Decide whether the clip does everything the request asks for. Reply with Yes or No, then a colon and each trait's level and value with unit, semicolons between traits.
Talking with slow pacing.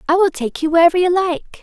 No: fast, 260 wpm